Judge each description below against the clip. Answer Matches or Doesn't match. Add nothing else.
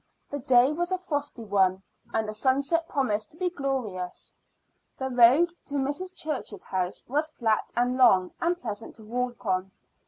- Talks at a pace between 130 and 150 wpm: Doesn't match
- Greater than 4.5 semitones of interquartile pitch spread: Matches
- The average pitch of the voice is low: Doesn't match